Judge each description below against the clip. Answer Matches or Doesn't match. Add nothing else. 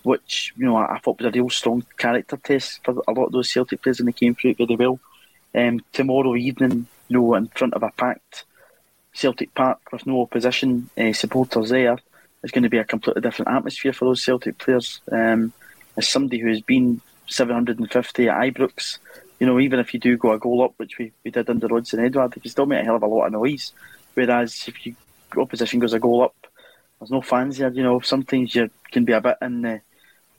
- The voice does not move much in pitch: Matches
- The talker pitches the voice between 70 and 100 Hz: Doesn't match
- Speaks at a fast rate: Matches